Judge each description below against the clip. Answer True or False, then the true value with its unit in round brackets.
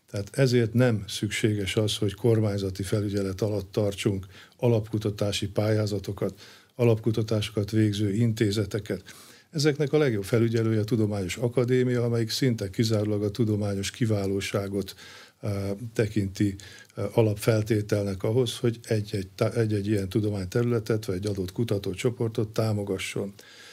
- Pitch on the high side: False (110 Hz)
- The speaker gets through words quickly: False (110 wpm)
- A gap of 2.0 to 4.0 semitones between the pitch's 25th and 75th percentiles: True (2.5 semitones)